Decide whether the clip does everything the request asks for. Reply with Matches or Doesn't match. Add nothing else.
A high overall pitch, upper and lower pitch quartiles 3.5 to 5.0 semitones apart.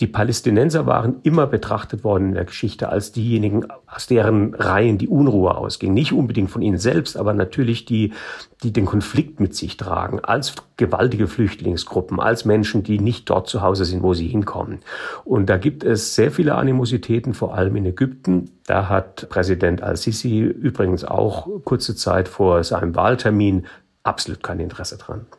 Doesn't match